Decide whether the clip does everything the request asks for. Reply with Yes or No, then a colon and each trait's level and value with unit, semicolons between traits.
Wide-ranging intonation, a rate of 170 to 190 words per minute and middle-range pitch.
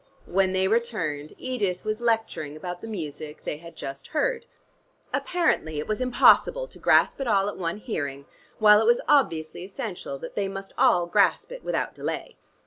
No: wide, 6.7 semitones; average, 175 wpm; high, 195 Hz